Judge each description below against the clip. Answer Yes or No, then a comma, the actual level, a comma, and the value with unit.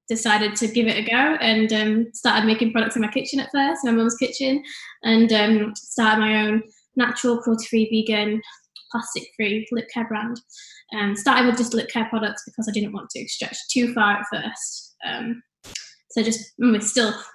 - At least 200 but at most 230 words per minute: No, average, 185 wpm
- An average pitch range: No, narrow, 1.9 semitones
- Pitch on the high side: Yes, high, 230 Hz